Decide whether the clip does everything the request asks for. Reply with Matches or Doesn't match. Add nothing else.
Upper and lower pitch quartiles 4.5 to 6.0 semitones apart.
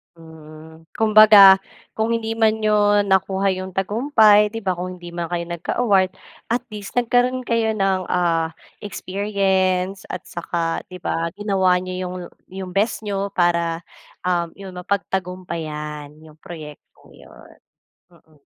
Doesn't match